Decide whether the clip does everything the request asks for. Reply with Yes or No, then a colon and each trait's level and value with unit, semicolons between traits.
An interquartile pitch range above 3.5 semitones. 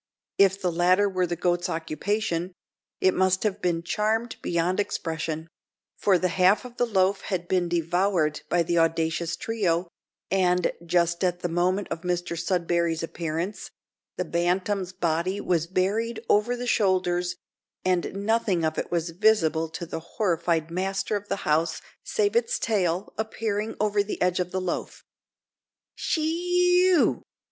No: average, 3.2 semitones